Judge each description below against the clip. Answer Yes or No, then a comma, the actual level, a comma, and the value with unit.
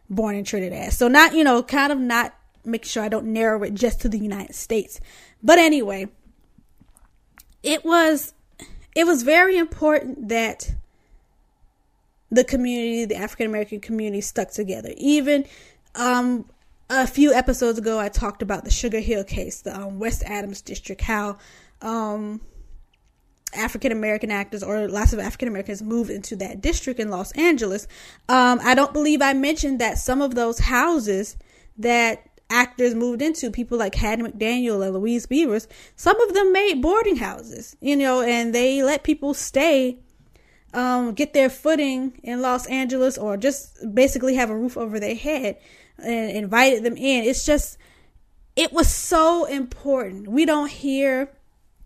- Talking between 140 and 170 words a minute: Yes, average, 160 wpm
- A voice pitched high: Yes, high, 245 Hz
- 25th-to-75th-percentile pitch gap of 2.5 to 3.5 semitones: No, average, 4.4 semitones